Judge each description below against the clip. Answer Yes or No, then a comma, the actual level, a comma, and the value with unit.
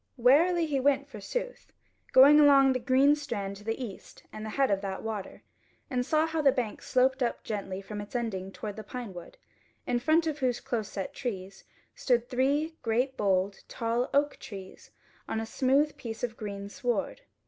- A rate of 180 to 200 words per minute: Yes, average, 185 wpm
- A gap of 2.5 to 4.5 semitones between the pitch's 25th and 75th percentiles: No, average, 5.0 semitones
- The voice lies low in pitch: No, high, 245 Hz